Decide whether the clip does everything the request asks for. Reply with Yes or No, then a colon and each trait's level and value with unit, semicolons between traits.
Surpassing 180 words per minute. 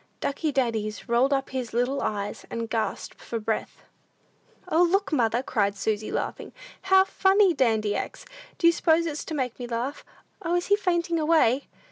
No: average, 170 wpm